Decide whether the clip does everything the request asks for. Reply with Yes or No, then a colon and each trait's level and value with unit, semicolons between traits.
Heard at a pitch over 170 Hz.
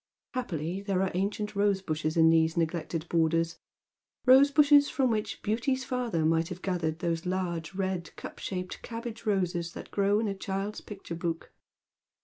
Yes: medium, 185 Hz